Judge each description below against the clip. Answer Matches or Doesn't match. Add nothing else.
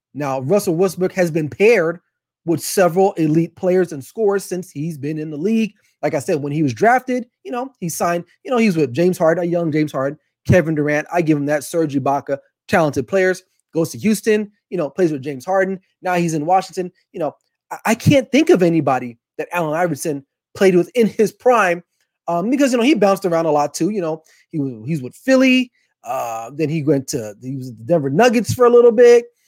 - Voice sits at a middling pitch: Matches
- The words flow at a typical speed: Doesn't match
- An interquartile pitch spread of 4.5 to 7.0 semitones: Matches